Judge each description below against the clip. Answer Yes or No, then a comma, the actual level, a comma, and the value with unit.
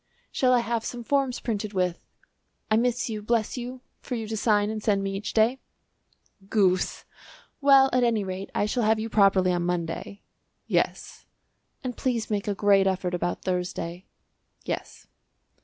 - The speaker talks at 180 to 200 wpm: No, average, 165 wpm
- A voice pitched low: No, high, 215 Hz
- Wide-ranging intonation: No, average, 3.6 semitones